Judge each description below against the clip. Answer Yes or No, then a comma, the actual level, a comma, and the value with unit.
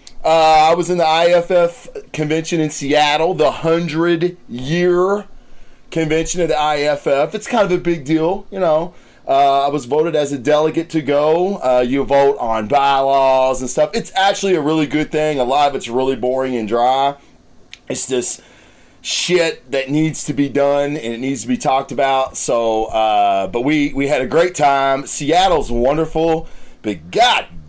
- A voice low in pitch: No, medium, 150 Hz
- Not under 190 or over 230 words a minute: No, average, 175 wpm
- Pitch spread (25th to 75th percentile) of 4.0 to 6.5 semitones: No, average, 3.5 semitones